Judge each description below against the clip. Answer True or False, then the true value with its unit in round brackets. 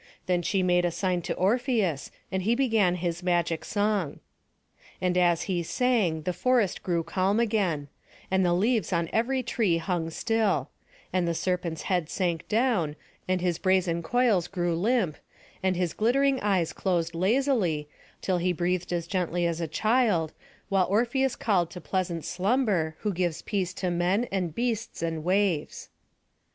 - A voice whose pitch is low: False (185 Hz)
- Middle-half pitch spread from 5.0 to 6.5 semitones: False (3.9 semitones)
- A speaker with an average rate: True (160 wpm)